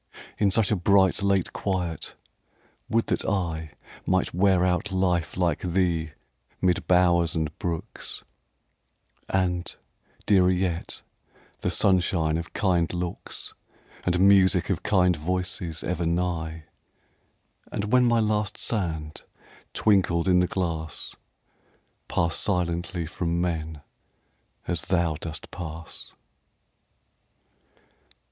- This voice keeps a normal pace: No, slow, 110 wpm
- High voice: No, very low, 90 Hz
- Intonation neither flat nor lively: No, narrow, 2.2 semitones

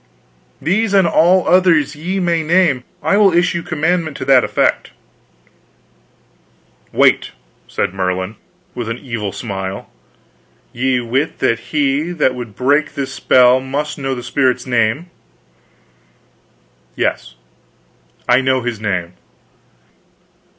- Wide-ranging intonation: Yes, wide, 5.7 semitones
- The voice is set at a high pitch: No, low, 135 Hz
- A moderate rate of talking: No, slow, 115 wpm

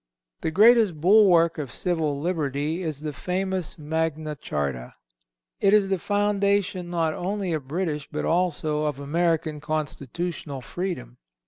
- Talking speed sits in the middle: No, slow, 130 wpm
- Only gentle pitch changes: No, average, 3.7 semitones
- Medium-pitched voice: Yes, medium, 165 Hz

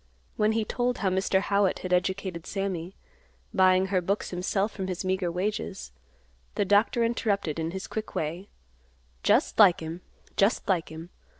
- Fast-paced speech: No, average, 160 wpm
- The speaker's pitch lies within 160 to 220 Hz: Yes, high, 190 Hz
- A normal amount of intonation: No, narrow, 2.3 semitones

